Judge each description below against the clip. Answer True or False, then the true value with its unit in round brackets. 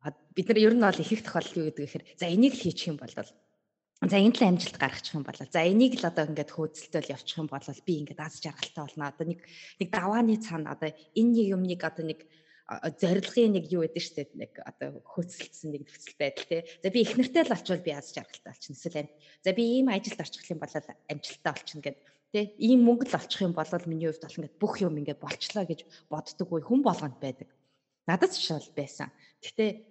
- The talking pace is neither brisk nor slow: False (220 wpm)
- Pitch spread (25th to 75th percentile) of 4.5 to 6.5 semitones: True (4.9 semitones)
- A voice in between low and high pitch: True (165 Hz)